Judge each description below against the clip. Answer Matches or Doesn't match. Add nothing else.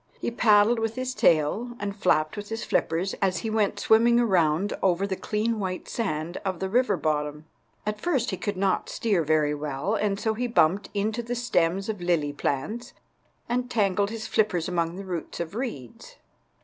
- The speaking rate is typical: Matches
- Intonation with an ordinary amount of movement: Matches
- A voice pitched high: Matches